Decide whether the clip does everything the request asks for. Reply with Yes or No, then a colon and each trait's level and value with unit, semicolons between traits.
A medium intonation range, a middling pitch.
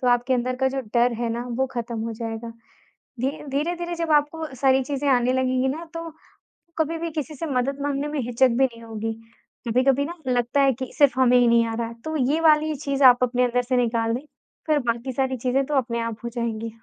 No: average, 3.0 semitones; very high, 255 Hz